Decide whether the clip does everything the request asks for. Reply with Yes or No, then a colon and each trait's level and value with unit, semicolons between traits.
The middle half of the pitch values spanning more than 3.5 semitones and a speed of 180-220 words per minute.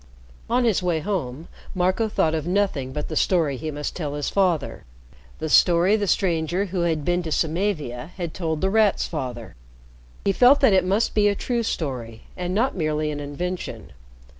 Yes: average, 4.5 semitones; average, 185 wpm